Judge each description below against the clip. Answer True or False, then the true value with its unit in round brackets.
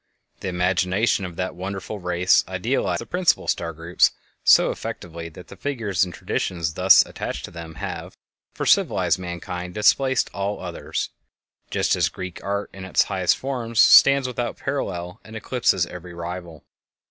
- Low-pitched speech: True (90 Hz)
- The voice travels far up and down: False (3.4 semitones)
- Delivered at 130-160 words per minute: True (155 wpm)